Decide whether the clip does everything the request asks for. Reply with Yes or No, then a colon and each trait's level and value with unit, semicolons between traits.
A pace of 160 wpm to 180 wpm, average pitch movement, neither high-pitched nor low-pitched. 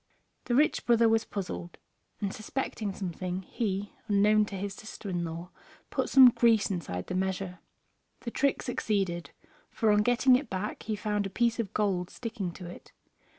No: average, 170 wpm; average, 3.5 semitones; high, 205 Hz